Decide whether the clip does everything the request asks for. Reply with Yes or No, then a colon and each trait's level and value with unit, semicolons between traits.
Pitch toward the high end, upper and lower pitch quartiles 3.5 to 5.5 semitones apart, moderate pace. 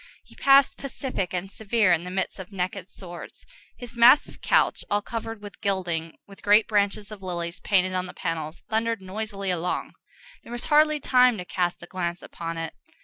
Yes: high, 195 Hz; average, 3.9 semitones; average, 185 wpm